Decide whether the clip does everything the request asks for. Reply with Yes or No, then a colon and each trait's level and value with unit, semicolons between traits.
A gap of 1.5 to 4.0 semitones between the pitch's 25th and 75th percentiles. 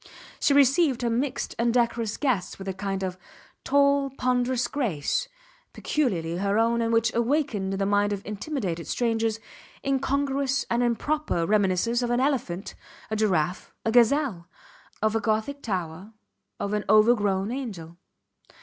No: average, 4.9 semitones